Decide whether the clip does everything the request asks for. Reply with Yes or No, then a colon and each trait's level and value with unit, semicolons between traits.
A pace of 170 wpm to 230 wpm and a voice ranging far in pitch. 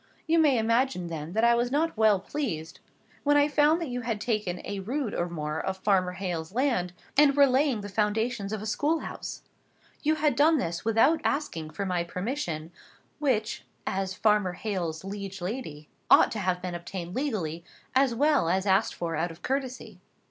Yes: average, 185 wpm; wide, 6.9 semitones